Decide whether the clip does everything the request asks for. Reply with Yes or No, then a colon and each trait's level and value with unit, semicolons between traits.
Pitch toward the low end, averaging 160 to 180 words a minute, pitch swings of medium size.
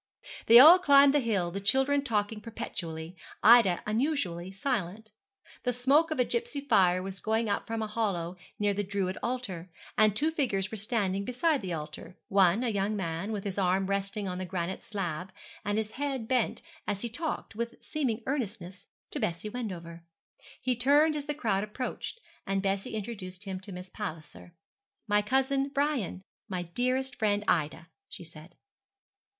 No: high, 210 Hz; average, 170 wpm; average, 5.0 semitones